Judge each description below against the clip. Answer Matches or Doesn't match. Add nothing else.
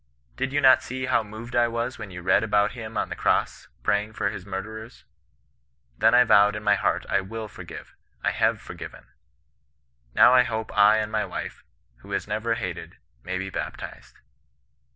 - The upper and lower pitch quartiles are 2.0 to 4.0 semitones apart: Matches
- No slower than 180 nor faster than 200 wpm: Matches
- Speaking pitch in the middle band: Doesn't match